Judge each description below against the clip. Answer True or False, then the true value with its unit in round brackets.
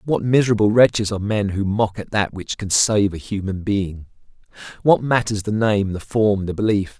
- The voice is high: False (105 Hz)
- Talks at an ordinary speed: True (195 wpm)